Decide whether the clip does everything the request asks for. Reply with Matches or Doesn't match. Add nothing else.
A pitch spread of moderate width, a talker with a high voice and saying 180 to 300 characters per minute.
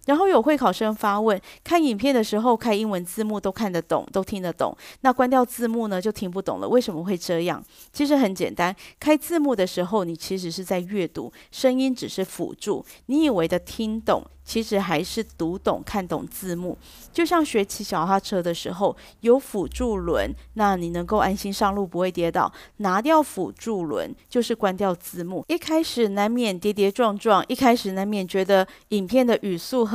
Matches